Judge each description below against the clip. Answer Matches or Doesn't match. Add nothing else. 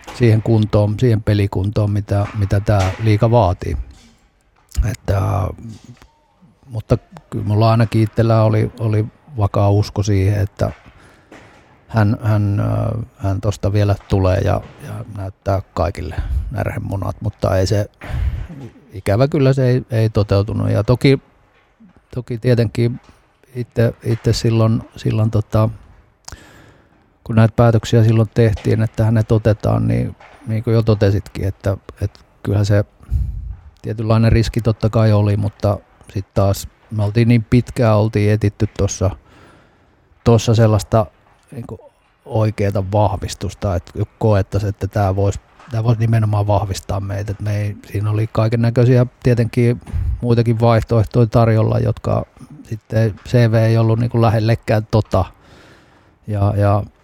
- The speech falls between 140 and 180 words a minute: Doesn't match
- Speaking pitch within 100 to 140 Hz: Matches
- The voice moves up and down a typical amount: Doesn't match